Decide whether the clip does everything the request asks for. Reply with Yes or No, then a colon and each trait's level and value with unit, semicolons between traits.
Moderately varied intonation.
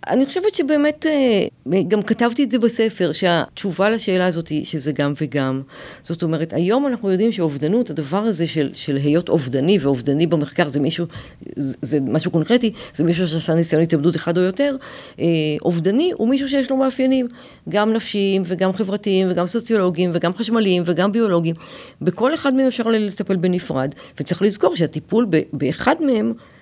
No: wide, 6.0 semitones